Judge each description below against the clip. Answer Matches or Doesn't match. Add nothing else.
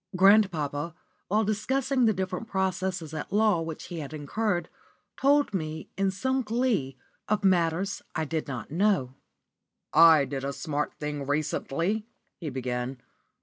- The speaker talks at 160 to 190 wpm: Doesn't match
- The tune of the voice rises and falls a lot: Matches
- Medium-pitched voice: Matches